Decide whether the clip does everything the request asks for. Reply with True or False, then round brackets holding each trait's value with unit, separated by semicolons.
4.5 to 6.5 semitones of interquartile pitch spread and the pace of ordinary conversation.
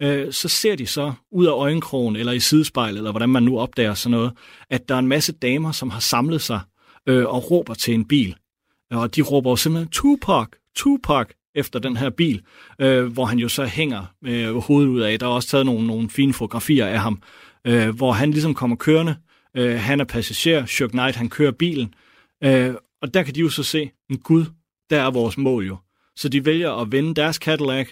False (4.1 semitones; 205 wpm)